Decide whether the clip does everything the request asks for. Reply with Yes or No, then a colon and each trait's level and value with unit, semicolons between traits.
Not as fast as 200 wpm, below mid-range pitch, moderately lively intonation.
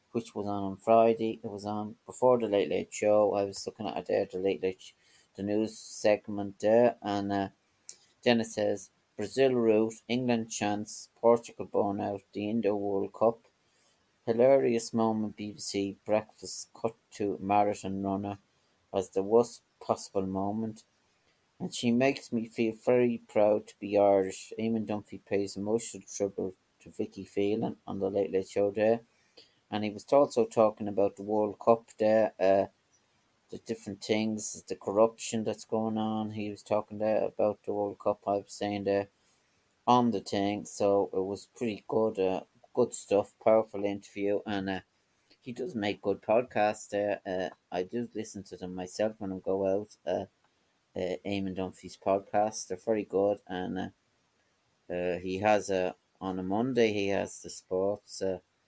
No: average, 170 wpm; low, 105 Hz; narrow, 2.1 semitones